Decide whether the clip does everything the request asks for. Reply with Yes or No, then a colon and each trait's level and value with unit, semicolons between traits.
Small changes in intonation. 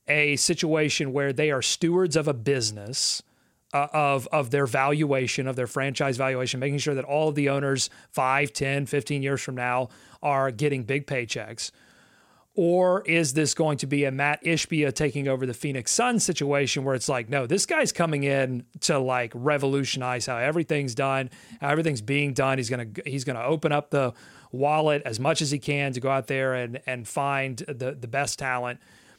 Yes: narrow, 2.1 semitones